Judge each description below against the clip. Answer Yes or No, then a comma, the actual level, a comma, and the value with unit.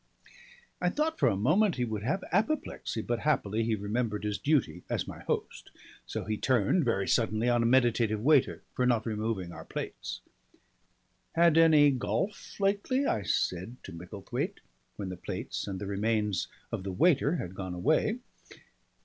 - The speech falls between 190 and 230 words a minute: No, average, 165 wpm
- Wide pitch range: Yes, wide, 7.1 semitones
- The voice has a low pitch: Yes, low, 115 Hz